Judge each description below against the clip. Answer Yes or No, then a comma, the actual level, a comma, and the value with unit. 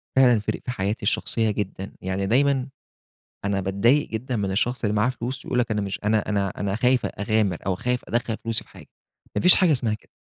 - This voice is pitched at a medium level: No, low, 110 Hz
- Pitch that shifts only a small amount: No, average, 3.7 semitones